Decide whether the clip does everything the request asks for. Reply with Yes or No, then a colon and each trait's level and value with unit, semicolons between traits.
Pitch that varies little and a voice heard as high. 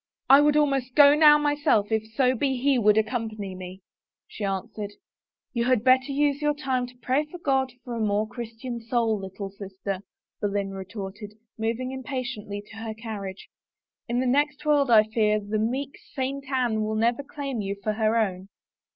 No: average, 4.1 semitones; high, 230 Hz